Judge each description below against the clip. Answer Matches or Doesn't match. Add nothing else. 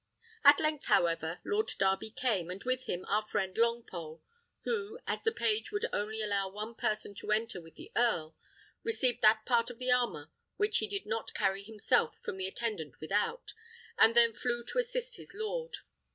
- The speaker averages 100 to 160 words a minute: Doesn't match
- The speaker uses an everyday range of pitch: Matches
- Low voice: Doesn't match